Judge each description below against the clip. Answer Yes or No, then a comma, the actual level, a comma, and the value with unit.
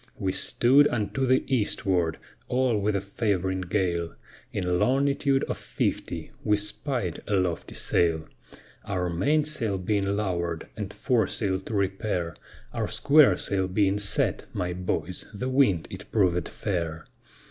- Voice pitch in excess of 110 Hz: No, low, 100 Hz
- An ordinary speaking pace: No, slow, 130 wpm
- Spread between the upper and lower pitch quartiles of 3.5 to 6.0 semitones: Yes, average, 4.3 semitones